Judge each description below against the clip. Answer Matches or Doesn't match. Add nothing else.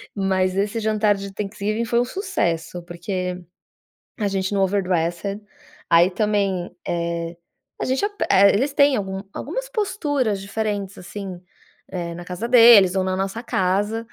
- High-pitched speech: Matches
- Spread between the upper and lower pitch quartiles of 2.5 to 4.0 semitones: Matches